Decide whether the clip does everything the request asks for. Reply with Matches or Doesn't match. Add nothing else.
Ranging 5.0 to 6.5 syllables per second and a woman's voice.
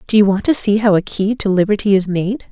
Matches